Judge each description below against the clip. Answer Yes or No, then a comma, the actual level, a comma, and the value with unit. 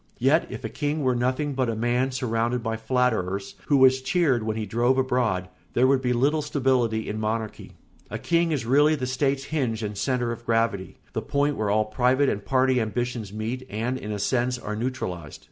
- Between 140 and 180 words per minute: No, average, 200 wpm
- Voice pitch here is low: Yes, low, 125 Hz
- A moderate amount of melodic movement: Yes, average, 3.1 semitones